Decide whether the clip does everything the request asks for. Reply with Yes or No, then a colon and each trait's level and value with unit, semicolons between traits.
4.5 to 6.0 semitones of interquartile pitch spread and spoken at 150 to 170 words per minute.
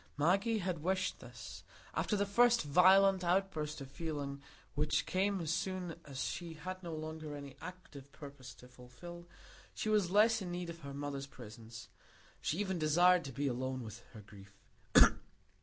Yes: average, 5.0 semitones; average, 165 wpm